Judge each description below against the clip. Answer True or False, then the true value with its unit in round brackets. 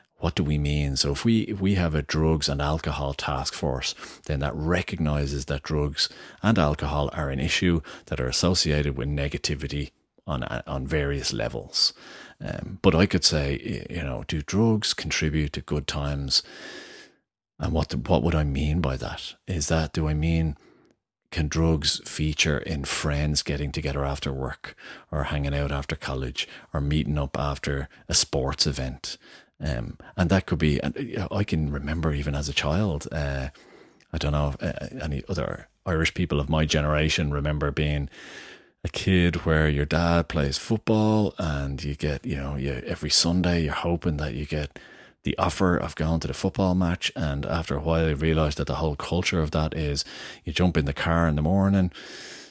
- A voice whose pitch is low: True (75 Hz)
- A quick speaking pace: False (180 wpm)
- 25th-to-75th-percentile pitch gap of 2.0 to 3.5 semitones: True (2.8 semitones)